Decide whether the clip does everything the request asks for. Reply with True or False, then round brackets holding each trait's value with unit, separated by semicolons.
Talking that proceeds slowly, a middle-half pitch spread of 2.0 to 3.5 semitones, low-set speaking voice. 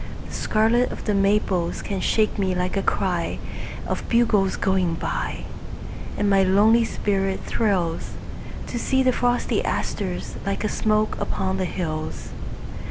False (130 wpm; 2.4 semitones; 200 Hz)